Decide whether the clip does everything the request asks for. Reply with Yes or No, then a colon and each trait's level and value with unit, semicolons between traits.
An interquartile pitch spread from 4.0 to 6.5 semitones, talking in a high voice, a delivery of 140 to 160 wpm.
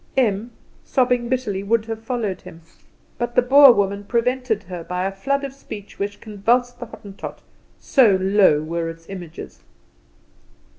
Yes: average, 4.3 semitones; high, 210 Hz; average, 150 wpm